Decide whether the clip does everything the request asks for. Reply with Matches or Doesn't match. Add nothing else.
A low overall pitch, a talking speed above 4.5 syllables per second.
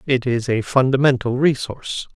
Matches